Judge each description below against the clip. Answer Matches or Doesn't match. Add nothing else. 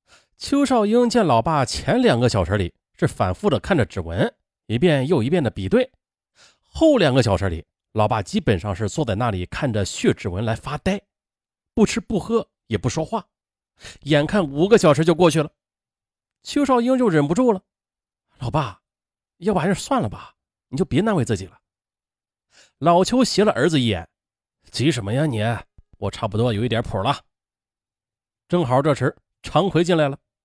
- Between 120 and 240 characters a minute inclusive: Doesn't match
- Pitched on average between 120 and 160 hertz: Matches